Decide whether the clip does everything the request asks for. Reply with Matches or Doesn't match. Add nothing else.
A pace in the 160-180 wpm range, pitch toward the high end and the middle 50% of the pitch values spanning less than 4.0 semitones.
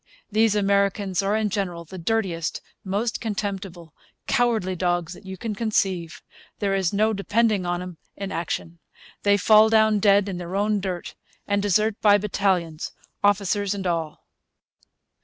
Doesn't match